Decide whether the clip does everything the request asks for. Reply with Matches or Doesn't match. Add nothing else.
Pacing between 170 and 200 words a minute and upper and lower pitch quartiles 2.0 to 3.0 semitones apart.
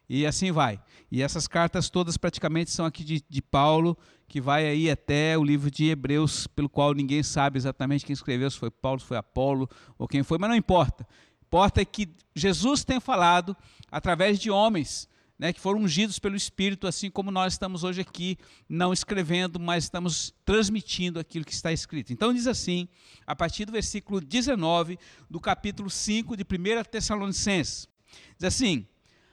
Doesn't match